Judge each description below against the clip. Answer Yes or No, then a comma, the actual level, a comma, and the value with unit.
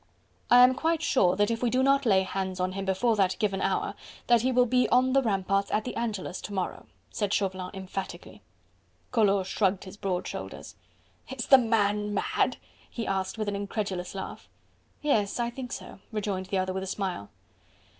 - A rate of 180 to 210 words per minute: Yes, average, 190 wpm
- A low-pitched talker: No, high, 205 Hz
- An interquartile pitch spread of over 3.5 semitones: Yes, average, 3.9 semitones